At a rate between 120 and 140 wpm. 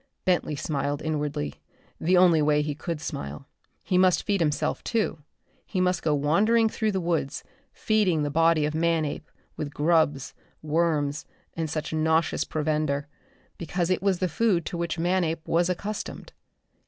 No: average, 155 wpm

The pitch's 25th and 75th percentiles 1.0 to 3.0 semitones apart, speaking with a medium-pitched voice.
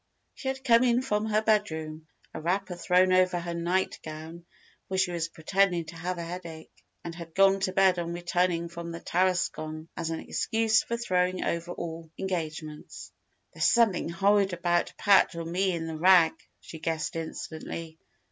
Yes: narrow, 2.5 semitones; medium, 175 Hz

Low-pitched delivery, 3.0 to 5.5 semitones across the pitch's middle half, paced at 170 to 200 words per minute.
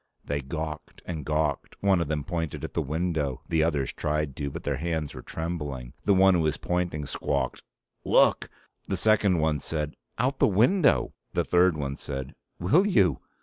Yes: very low, 80 Hz; average, 3.6 semitones; average, 180 wpm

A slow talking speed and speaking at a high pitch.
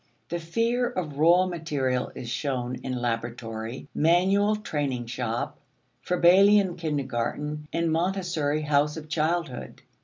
No: slow, 115 wpm; medium, 155 Hz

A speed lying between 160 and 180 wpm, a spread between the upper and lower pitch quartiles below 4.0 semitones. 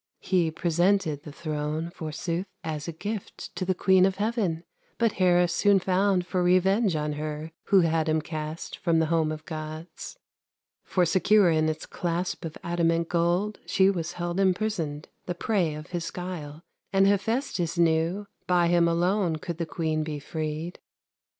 Yes: average, 165 wpm; average, 2.8 semitones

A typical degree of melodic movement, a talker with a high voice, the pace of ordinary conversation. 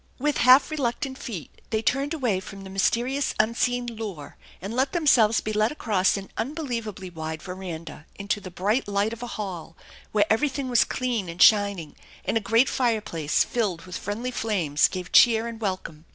Yes: average, 4.6 semitones; high, 215 Hz; average, 180 wpm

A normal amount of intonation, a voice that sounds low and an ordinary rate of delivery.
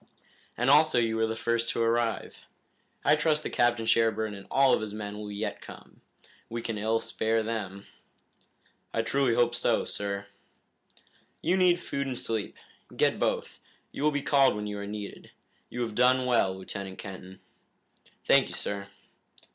Yes: average, 3.3 semitones; low, 115 Hz; average, 170 wpm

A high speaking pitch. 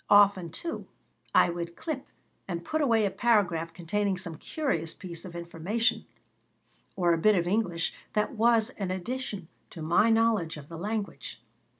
Yes: high, 195 Hz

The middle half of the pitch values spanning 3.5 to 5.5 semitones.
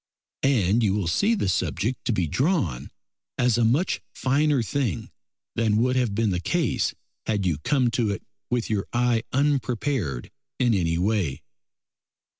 Yes: average, 5.1 semitones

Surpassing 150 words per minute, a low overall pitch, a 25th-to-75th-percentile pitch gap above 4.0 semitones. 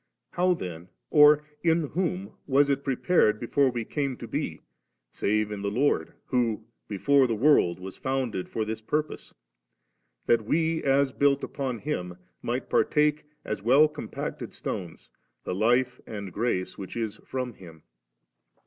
Yes: average, 160 wpm; low, 125 Hz; average, 5.2 semitones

